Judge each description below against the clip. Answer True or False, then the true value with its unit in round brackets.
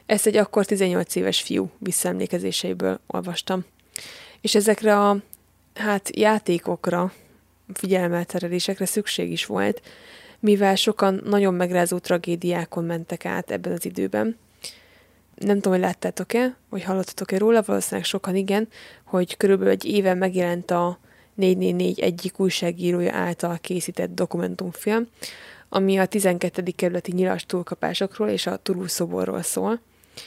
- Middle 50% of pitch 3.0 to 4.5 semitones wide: False (2.6 semitones)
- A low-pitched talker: False (185 Hz)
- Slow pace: False (115 wpm)